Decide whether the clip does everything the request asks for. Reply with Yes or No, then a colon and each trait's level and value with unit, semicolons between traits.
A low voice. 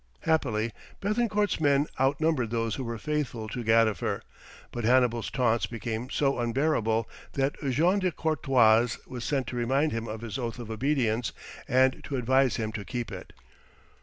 Yes: low, 125 Hz